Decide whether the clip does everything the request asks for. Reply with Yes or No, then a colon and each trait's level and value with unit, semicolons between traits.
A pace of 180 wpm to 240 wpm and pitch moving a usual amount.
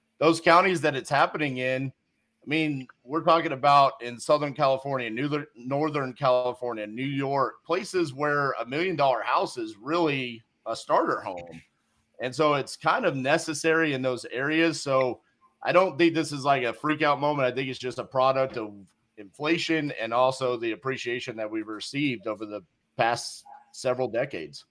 No: average, 170 wpm; average, 4.0 semitones